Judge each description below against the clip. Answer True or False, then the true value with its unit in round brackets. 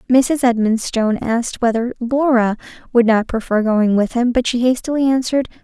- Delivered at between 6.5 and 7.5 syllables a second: False (5.3 syllables/s)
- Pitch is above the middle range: True (240 Hz)